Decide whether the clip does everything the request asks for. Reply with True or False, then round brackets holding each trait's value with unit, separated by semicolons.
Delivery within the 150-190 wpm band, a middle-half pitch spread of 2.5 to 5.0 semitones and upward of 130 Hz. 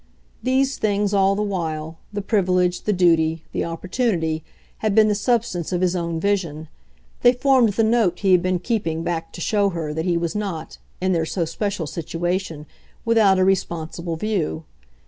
True (175 wpm; 3.9 semitones; 185 Hz)